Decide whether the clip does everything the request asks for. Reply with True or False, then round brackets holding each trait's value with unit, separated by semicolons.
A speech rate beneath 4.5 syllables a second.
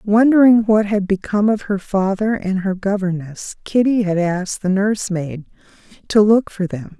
False (4.9 syllables/s)